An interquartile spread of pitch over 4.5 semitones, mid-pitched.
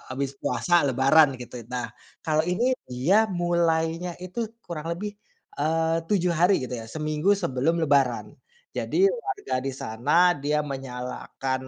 Yes: average, 5.0 semitones; medium, 155 Hz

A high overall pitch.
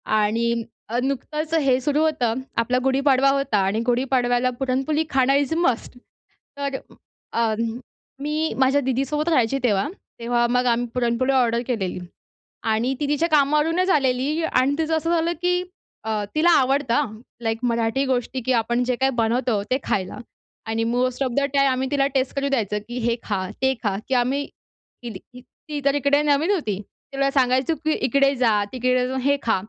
Yes: very high, 260 Hz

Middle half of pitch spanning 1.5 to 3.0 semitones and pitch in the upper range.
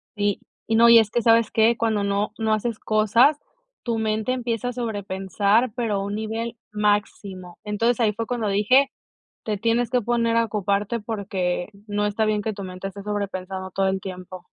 Yes: narrow, 2.5 semitones; high, 215 Hz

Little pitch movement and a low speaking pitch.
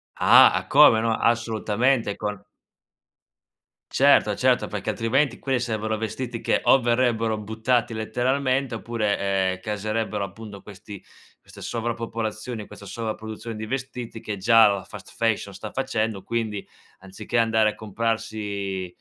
Yes: narrow, 2.1 semitones; low, 110 Hz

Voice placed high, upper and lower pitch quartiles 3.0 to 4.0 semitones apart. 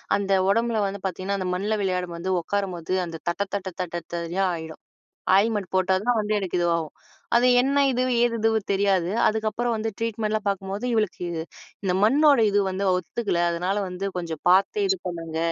Yes: high, 195 Hz; average, 3.5 semitones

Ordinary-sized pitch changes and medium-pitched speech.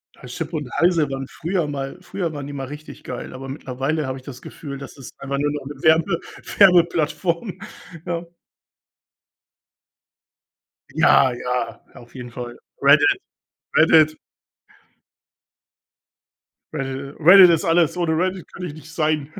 Yes: average, 3.8 semitones; medium, 155 Hz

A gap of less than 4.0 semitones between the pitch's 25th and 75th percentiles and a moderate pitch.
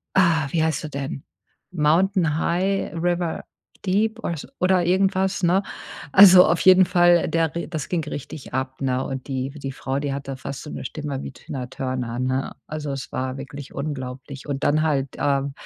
No: average, 4.4 semitones; medium, 150 Hz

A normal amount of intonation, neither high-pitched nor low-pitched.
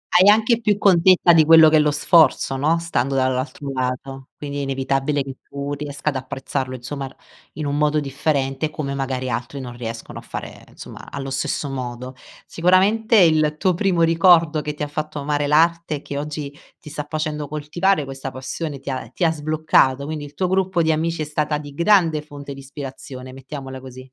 Yes: average, 3.1 semitones; medium, 145 Hz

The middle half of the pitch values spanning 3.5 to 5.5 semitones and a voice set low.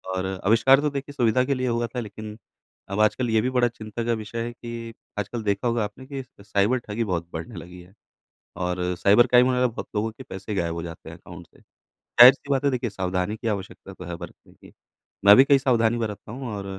Yes: average, 3.9 semitones; low, 115 Hz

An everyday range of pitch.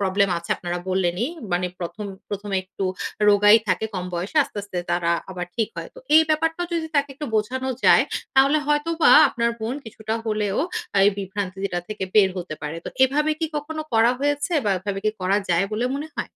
No: wide, 7.0 semitones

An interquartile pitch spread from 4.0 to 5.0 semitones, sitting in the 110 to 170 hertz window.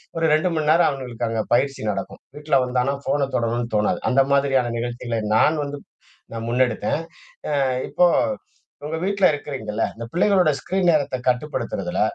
Yes: average, 4.3 semitones; low, 135 Hz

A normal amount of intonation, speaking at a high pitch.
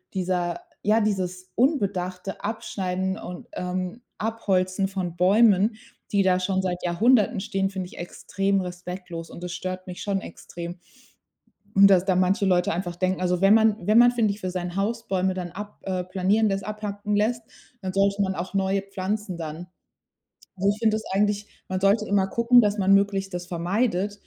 No: narrow, 2.2 semitones; high, 195 Hz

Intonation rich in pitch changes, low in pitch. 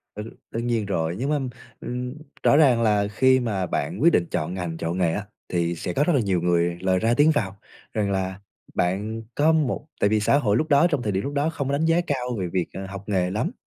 Yes: wide, 6.7 semitones; low, 105 Hz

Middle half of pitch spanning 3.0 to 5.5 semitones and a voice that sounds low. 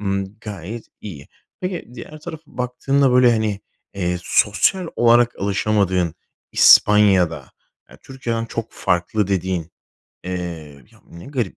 Yes: average, 5.1 semitones; low, 105 Hz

